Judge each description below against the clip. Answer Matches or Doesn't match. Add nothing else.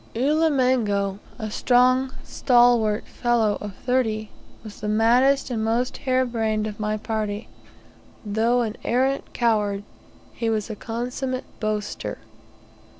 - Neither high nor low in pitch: Doesn't match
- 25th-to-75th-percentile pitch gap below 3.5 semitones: Matches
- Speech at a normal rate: Doesn't match